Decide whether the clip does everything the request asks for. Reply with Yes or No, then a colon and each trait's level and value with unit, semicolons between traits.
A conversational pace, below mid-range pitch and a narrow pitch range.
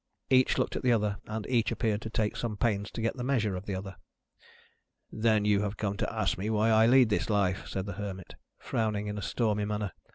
No: fast, 230 wpm; low, 105 Hz; narrow, 1.8 semitones